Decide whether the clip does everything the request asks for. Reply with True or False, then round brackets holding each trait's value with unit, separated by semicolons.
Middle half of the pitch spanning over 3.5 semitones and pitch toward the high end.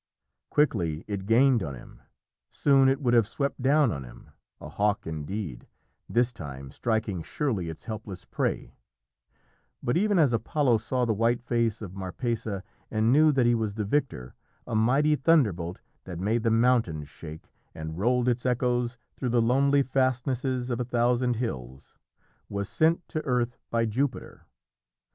False (4.4 semitones; 115 Hz)